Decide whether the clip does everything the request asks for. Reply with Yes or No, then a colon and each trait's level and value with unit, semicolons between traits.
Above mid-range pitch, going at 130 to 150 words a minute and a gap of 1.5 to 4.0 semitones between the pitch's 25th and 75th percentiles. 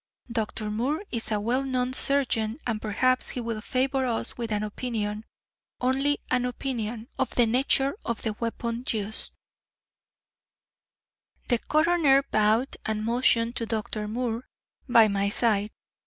Yes: high, 235 Hz; average, 140 wpm; average, 2.9 semitones